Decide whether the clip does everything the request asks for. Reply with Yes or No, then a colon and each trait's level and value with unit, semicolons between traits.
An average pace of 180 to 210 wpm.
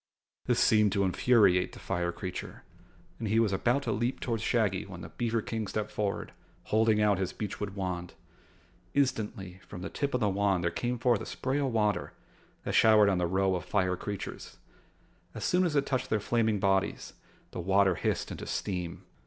Yes: average, 190 wpm